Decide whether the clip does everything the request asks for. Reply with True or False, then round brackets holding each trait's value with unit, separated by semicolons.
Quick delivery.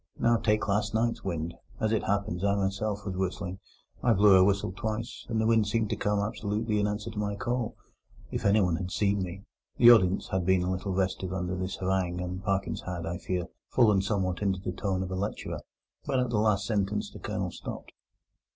True (210 wpm)